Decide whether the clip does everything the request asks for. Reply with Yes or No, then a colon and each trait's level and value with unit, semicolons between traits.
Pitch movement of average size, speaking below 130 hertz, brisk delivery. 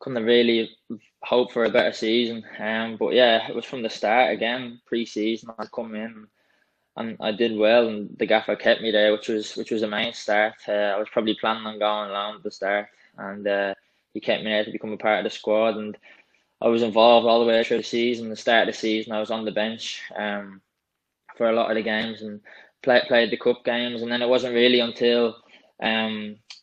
No: narrow, 1.7 semitones; low, 110 Hz; fast, 230 wpm